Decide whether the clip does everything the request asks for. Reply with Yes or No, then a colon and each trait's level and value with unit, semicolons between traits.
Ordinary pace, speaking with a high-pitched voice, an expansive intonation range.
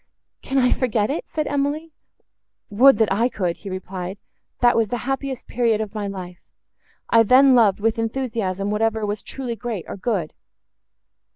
No: average, 155 wpm; high, 225 Hz; average, 4.0 semitones